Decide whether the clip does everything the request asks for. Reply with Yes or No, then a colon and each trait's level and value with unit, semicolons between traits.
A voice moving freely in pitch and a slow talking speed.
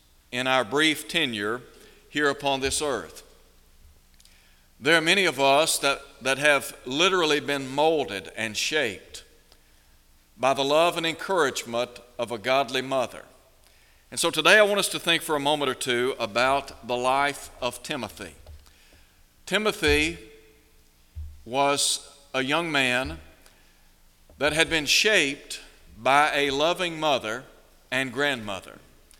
Yes: wide, 8.5 semitones; slow, 130 wpm